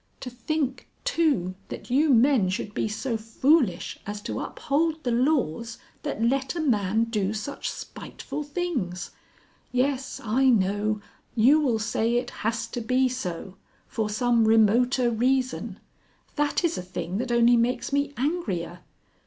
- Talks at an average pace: Yes, average, 145 wpm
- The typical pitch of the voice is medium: No, high, 240 Hz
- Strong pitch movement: No, average, 4.1 semitones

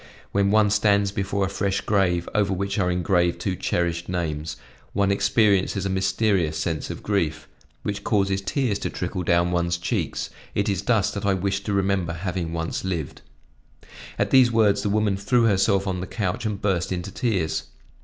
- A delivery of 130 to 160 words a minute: No, average, 180 wpm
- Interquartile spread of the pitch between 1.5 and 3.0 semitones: Yes, narrow, 2.4 semitones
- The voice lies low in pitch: Yes, very low, 95 Hz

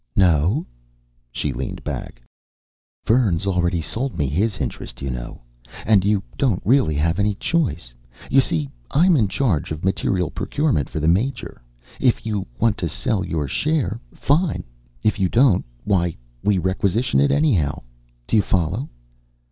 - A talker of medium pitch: No, very low, 95 Hz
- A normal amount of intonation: No, wide, 6.7 semitones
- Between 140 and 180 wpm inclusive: Yes, average, 150 wpm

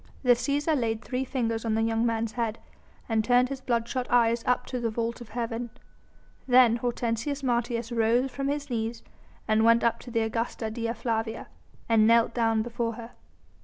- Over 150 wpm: Yes, average, 180 wpm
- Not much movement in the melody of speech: Yes, narrow, 1.5 semitones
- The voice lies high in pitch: Yes, high, 235 Hz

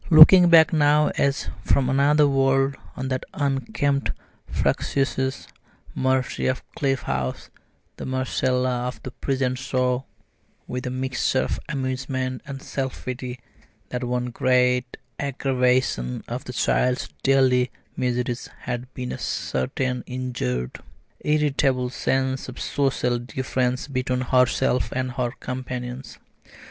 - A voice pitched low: Yes, low, 130 Hz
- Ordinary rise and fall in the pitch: No, narrow, 1.3 semitones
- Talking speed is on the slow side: Yes, slow, 120 wpm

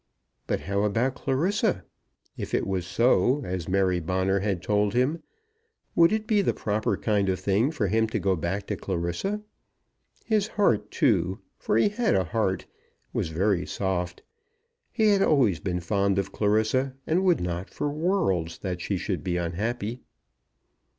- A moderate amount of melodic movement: No, wide, 6.5 semitones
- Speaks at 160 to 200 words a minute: Yes, average, 165 wpm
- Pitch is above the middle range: No, low, 105 Hz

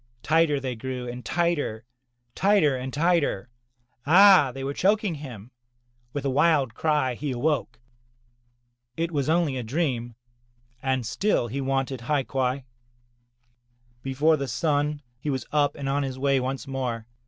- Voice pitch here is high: No, low, 135 Hz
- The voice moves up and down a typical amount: Yes, average, 3.1 semitones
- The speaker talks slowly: No, average, 145 wpm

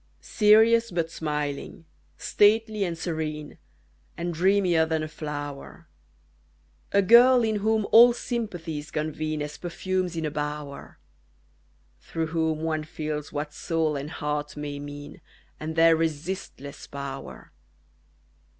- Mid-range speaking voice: Yes, medium, 160 Hz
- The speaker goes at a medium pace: No, slow, 120 wpm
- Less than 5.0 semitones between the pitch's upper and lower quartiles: Yes, average, 4.0 semitones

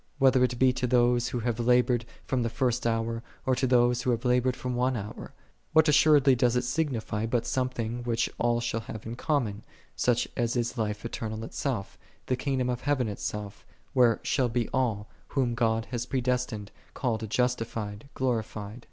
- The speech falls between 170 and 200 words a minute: Yes, average, 180 wpm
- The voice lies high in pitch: No, low, 120 Hz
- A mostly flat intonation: Yes, narrow, 2.0 semitones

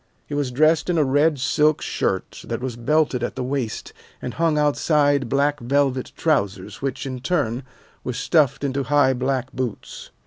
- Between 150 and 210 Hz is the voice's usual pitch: No, medium, 140 Hz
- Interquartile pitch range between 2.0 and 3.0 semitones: Yes, average, 2.7 semitones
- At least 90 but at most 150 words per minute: No, average, 170 wpm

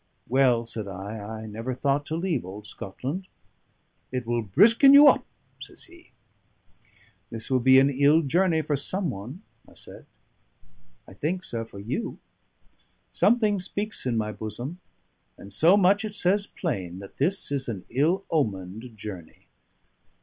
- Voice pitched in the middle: No, low, 130 Hz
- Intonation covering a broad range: Yes, wide, 8.8 semitones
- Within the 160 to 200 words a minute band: No, average, 150 wpm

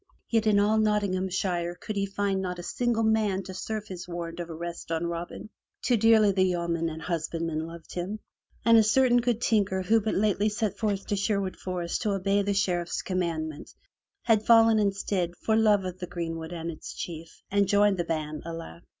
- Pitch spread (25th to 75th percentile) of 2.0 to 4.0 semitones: Yes, average, 3.7 semitones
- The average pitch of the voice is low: No, high, 190 Hz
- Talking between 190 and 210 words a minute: Yes, average, 195 wpm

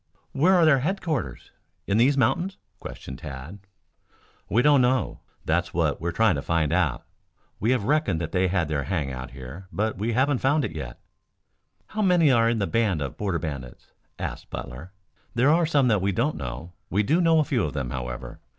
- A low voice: Yes, low, 100 Hz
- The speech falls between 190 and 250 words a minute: Yes, average, 195 wpm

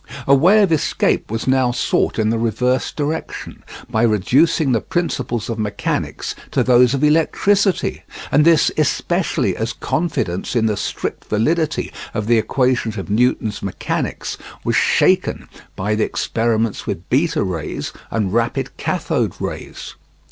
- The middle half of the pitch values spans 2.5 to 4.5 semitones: No, wide, 5.4 semitones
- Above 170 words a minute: No, average, 140 wpm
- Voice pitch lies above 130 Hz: No, low, 120 Hz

